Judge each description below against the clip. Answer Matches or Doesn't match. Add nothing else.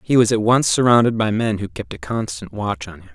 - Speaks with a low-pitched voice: Matches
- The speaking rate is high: Matches